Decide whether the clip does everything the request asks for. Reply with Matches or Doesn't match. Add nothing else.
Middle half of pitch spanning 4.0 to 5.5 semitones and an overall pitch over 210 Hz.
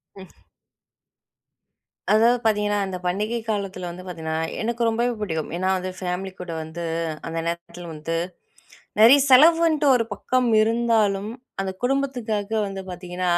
Doesn't match